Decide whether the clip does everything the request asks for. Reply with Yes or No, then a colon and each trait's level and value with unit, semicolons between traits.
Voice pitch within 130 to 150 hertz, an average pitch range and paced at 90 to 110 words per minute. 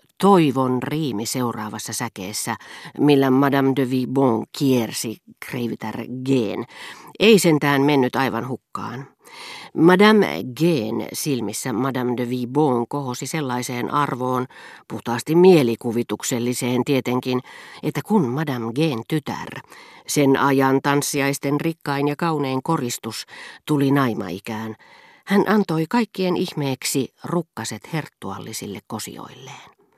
Yes: low, 135 Hz; average, 3.9 semitones; average, 100 wpm